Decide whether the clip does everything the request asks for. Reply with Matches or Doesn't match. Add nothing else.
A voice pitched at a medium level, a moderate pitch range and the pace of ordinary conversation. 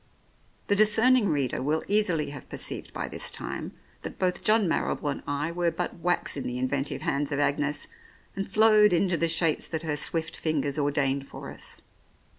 Matches